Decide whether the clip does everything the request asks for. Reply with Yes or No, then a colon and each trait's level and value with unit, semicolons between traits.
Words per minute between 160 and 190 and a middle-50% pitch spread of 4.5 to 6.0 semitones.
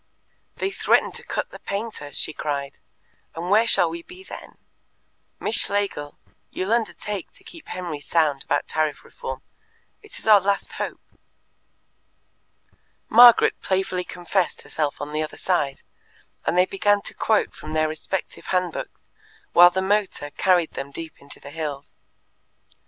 No: average, 150 wpm; average, 5.0 semitones